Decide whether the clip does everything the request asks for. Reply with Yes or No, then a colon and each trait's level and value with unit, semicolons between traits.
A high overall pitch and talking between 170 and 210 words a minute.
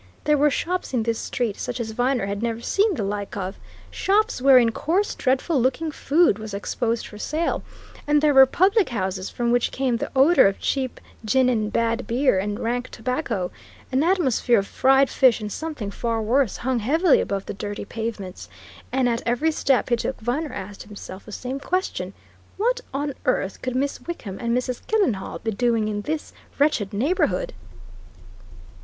Yes: high, 245 Hz; average, 180 wpm